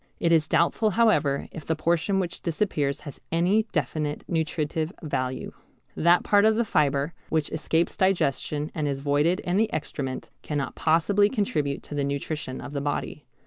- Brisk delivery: No, average, 165 wpm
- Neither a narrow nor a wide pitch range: Yes, average, 3.7 semitones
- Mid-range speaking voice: Yes, medium, 160 Hz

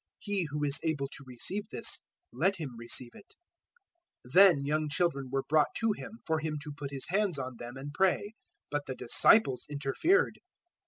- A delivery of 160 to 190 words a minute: Yes, average, 180 wpm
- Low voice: No, medium, 150 Hz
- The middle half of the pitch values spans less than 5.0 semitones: No, wide, 5.5 semitones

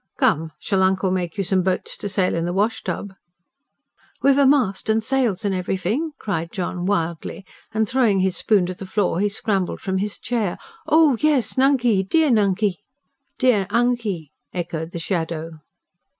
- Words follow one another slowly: No, average, 165 wpm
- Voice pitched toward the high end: Yes, high, 195 Hz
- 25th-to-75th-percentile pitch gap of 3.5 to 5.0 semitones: Yes, average, 4.1 semitones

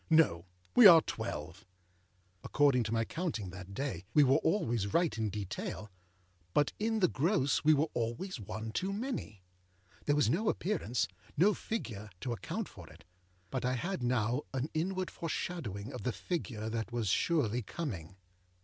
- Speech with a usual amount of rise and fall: No, wide, 7.5 semitones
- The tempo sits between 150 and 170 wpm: Yes, average, 155 wpm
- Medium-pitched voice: No, low, 125 Hz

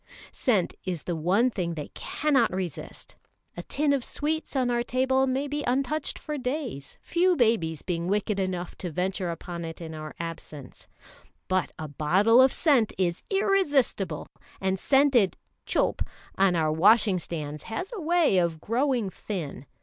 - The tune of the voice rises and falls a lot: Yes, wide, 7.7 semitones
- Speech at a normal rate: Yes, average, 155 wpm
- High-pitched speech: Yes, high, 200 Hz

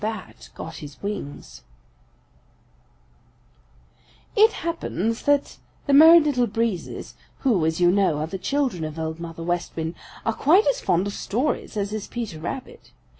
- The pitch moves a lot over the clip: Yes, wide, 8.8 semitones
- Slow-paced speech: No, average, 150 wpm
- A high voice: Yes, high, 205 Hz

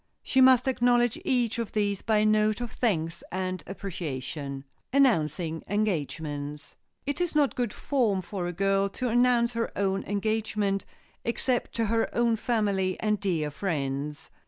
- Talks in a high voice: Yes, high, 205 Hz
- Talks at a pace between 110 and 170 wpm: Yes, average, 155 wpm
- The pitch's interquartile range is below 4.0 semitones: No, average, 5.2 semitones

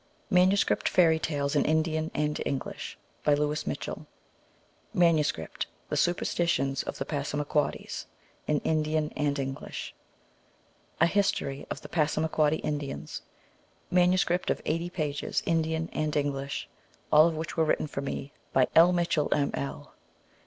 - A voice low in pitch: No, medium, 155 Hz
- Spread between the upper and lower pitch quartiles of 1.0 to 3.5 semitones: Yes, narrow, 2.4 semitones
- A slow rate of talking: Yes, slow, 130 wpm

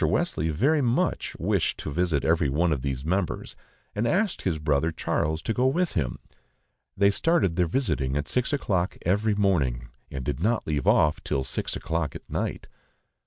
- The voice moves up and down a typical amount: No, wide, 6.7 semitones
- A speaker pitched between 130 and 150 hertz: No, very low, 85 Hz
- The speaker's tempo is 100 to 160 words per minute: No, average, 175 wpm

